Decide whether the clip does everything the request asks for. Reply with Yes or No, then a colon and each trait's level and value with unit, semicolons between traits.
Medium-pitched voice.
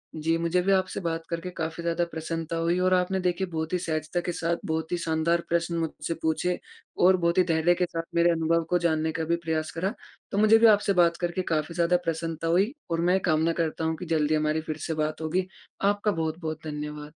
Yes: medium, 165 Hz